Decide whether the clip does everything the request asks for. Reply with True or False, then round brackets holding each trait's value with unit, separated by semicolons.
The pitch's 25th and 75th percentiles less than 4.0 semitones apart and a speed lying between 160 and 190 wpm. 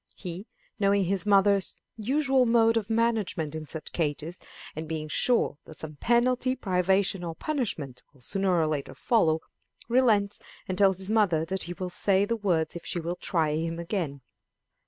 False (5.2 semitones; 170 wpm)